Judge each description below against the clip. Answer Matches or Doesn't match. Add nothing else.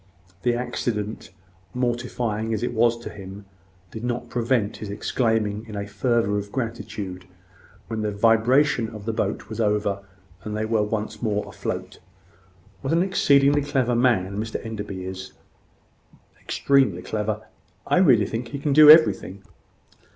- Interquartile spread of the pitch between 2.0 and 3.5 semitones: Matches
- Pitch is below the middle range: Matches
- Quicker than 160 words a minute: Doesn't match